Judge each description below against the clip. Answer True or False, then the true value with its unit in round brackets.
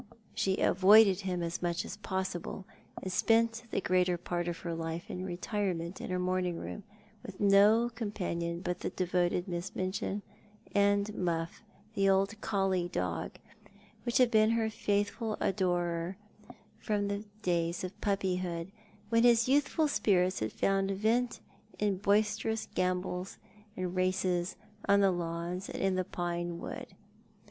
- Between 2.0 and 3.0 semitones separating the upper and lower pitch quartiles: True (2.7 semitones)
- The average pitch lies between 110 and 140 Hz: False (185 Hz)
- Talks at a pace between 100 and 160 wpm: True (145 wpm)